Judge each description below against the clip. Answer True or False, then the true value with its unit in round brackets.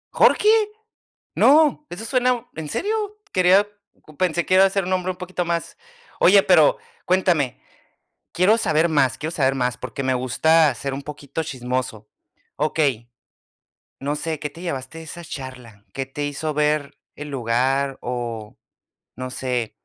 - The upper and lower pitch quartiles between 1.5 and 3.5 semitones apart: False (5.4 semitones)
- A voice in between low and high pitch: True (150 Hz)